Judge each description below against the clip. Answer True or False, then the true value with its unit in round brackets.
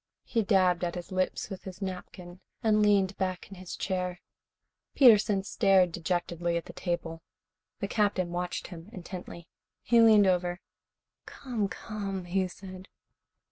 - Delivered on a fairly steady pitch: True (2.2 semitones)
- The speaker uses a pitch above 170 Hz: True (185 Hz)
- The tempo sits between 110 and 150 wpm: True (140 wpm)